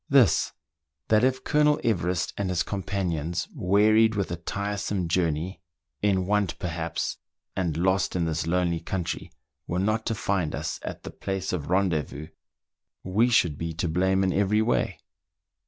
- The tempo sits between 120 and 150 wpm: No, average, 160 wpm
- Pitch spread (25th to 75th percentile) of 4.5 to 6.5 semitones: No, average, 3.4 semitones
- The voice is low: Yes, very low, 95 Hz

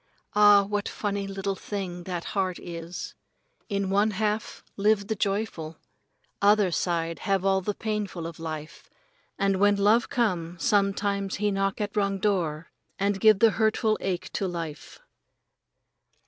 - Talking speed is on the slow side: No, average, 150 wpm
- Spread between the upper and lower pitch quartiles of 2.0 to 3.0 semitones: Yes, narrow, 2.6 semitones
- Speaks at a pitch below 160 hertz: No, high, 195 Hz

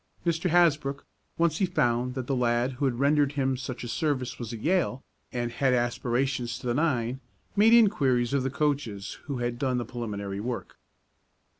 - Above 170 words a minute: Yes, average, 180 wpm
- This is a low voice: Yes, low, 130 Hz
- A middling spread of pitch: Yes, average, 3.2 semitones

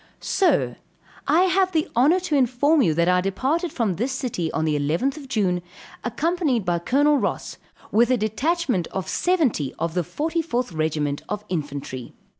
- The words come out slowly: No, average, 160 wpm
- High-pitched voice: Yes, high, 240 Hz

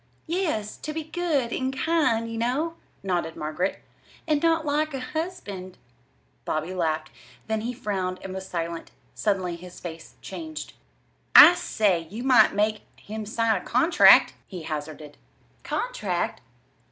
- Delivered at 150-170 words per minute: No, average, 140 wpm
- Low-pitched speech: No, high, 220 Hz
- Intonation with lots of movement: Yes, wide, 8.6 semitones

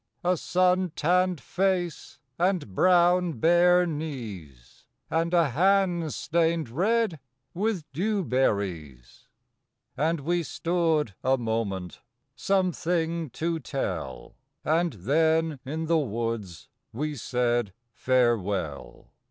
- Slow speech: Yes, slow, 100 wpm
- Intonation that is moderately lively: No, wide, 6.9 semitones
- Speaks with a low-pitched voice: No, medium, 160 Hz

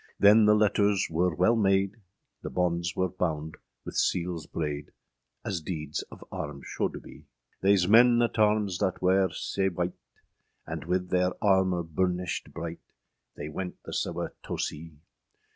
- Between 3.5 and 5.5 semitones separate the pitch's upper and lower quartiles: No, average, 2.9 semitones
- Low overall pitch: Yes, very low, 90 Hz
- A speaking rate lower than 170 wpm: Yes, average, 155 wpm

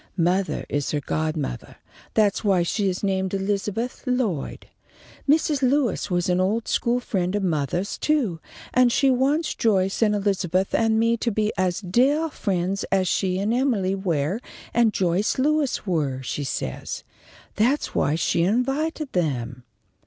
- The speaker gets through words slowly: No, average, 150 wpm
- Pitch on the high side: Yes, high, 195 Hz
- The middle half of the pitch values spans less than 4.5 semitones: No, average, 5.2 semitones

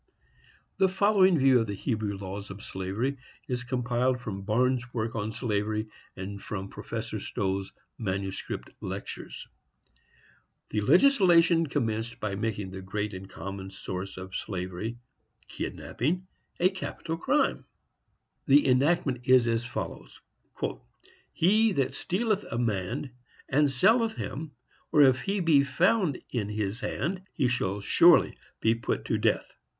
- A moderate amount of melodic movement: No, wide, 6.9 semitones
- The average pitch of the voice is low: Yes, low, 120 Hz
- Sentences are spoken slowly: Yes, slow, 130 wpm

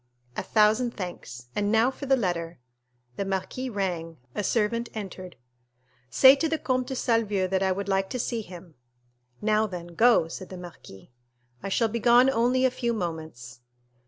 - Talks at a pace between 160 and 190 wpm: Yes, average, 170 wpm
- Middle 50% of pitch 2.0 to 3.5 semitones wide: No, average, 4.9 semitones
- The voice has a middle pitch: No, high, 205 Hz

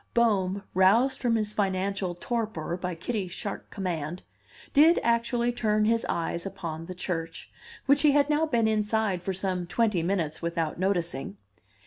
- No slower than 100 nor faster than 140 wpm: No, average, 150 wpm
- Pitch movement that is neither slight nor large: Yes, average, 4.7 semitones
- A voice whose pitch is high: Yes, high, 195 Hz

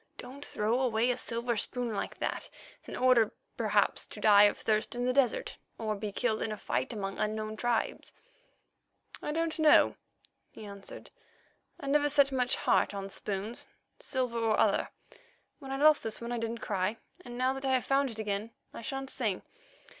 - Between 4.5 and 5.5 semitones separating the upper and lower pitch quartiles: No, average, 3.6 semitones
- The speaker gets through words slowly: No, average, 185 wpm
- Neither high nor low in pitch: No, high, 235 Hz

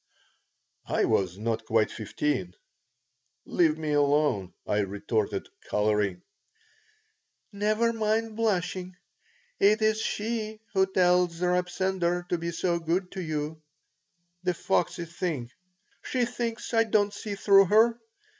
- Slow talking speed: Yes, slow, 120 wpm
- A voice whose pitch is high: No, medium, 180 Hz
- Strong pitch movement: Yes, wide, 6.1 semitones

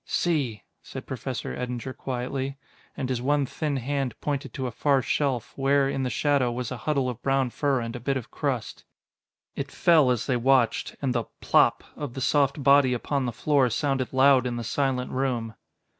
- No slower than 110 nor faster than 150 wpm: No, average, 190 wpm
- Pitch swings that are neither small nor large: No, narrow, 2.1 semitones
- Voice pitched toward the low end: Yes, low, 130 Hz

